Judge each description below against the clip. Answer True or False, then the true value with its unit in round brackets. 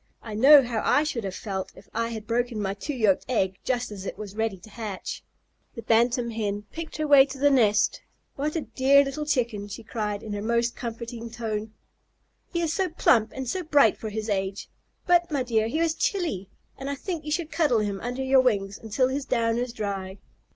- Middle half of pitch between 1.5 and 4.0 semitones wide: False (4.6 semitones)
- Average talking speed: False (215 wpm)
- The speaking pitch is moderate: False (235 Hz)